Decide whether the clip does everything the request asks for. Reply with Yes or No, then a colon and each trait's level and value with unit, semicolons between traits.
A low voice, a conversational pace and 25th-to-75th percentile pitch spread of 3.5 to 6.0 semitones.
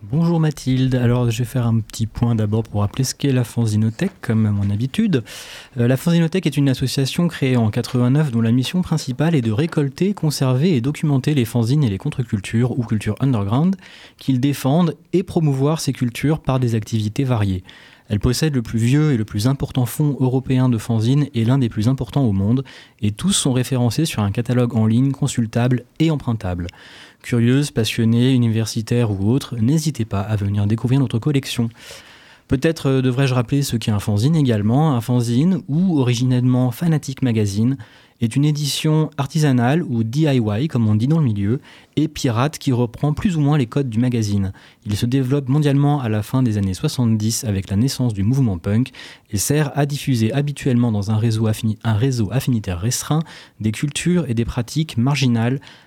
Yes: low, 125 Hz; average, 185 wpm; average, 3.8 semitones